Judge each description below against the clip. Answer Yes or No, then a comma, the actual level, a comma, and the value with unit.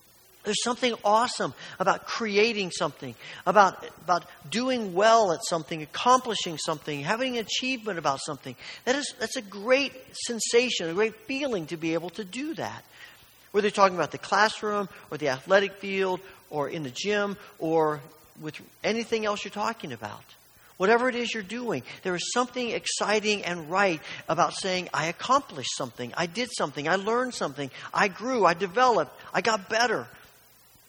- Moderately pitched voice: No, high, 200 Hz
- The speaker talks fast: No, average, 165 wpm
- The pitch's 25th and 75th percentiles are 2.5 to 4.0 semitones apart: No, wide, 5.5 semitones